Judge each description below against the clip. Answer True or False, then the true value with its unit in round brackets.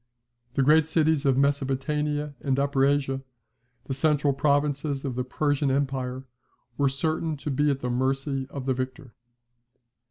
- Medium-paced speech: True (150 wpm)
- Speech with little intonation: True (1.8 semitones)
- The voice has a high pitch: False (140 Hz)